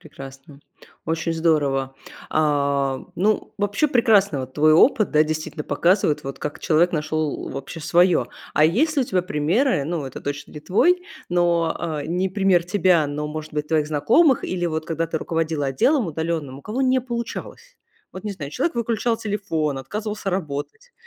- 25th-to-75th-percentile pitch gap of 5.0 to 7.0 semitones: Yes, wide, 5.4 semitones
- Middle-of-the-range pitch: Yes, medium, 165 Hz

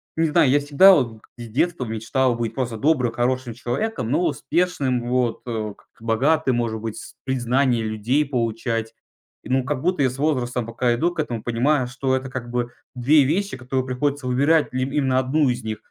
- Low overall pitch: Yes, low, 130 Hz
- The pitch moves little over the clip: No, average, 3.2 semitones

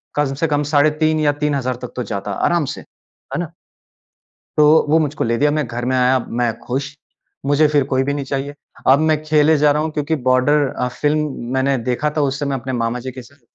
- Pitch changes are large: No, average, 2.8 semitones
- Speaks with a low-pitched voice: No, medium, 145 Hz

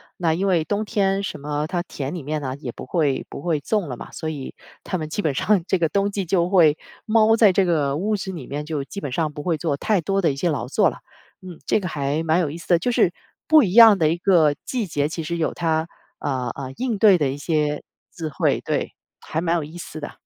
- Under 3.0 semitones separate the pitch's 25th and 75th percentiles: No, average, 4.5 semitones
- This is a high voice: No, medium, 165 Hz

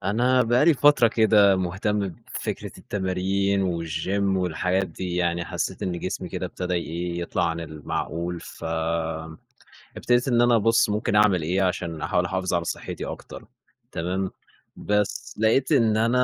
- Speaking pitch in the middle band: No, very low, 95 Hz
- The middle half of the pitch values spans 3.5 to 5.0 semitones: Yes, average, 3.9 semitones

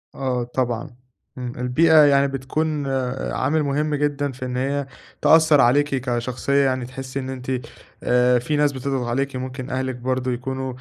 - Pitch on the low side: Yes, low, 130 Hz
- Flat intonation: Yes, narrow, 2.0 semitones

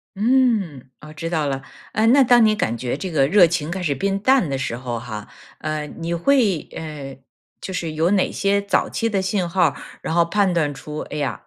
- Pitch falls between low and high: Yes, medium, 170 Hz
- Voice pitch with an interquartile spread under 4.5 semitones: No, wide, 5.4 semitones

